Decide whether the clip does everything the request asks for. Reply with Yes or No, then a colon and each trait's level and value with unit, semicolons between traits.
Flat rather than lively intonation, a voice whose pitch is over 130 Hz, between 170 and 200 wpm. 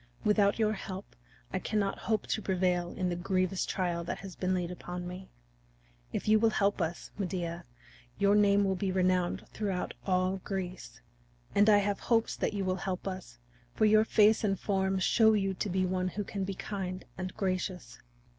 Yes: narrow, 1.9 semitones; high, 190 Hz; average, 185 wpm